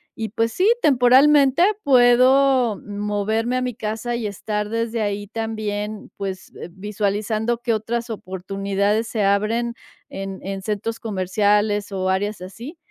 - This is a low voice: No, high, 215 Hz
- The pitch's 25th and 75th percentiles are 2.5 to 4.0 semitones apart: Yes, average, 2.8 semitones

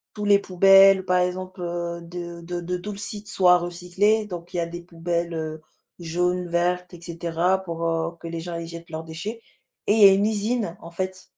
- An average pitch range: No, narrow, 2.1 semitones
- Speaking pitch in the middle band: Yes, medium, 175 Hz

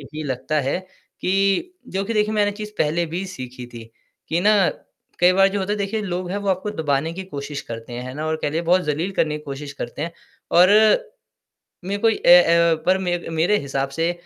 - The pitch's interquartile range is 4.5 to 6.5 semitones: Yes, average, 4.9 semitones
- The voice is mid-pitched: Yes, medium, 170 Hz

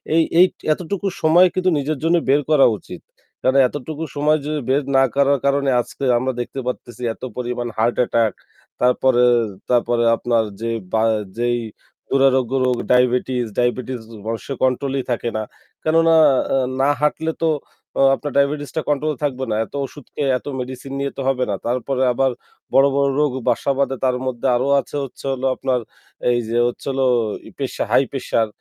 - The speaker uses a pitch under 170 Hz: Yes, low, 135 Hz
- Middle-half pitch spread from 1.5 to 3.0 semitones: Yes, average, 2.7 semitones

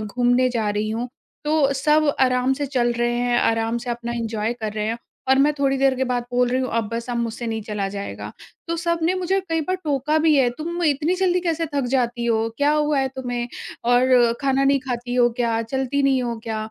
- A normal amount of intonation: Yes, average, 3.2 semitones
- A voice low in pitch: No, very high, 250 Hz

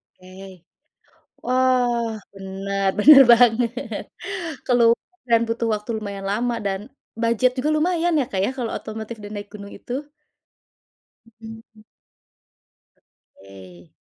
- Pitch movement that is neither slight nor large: Yes, average, 3.7 semitones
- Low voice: No, high, 225 Hz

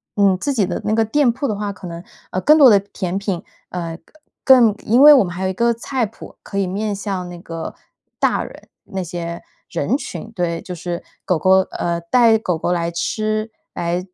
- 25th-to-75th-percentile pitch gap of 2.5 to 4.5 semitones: Yes, average, 4.1 semitones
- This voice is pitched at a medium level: No, high, 195 Hz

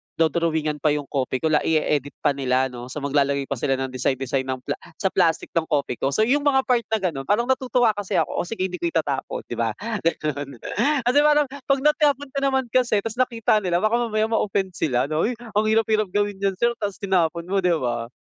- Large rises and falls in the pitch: Yes, wide, 8.1 semitones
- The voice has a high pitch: No, medium, 180 Hz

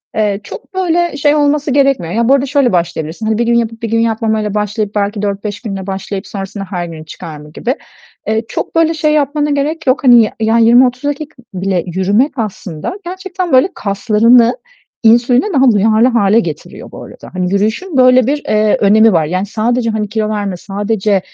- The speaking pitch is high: Yes, high, 220 Hz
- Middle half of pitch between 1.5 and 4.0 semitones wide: No, average, 4.8 semitones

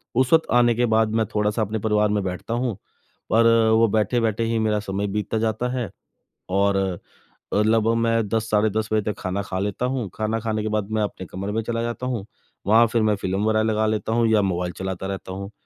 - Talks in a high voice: No, low, 110 Hz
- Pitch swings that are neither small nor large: No, narrow, 2.2 semitones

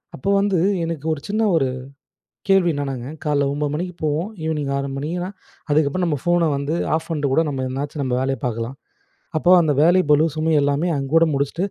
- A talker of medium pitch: Yes, medium, 150 Hz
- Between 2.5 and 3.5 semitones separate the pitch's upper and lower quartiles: Yes, average, 3.2 semitones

